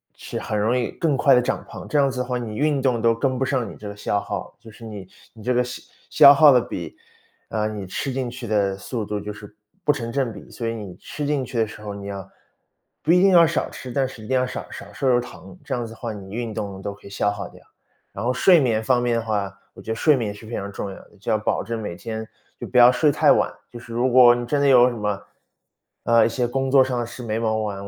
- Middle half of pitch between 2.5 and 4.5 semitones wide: Yes, average, 3.5 semitones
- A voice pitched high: No, low, 115 Hz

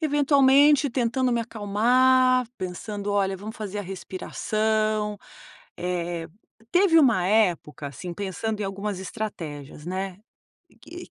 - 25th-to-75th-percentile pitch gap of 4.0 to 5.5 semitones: Yes, average, 5.2 semitones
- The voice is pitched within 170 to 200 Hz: No, high, 210 Hz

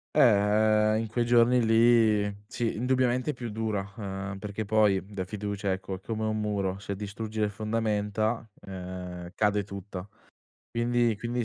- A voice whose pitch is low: Yes, low, 105 Hz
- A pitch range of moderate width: No, narrow, 2.2 semitones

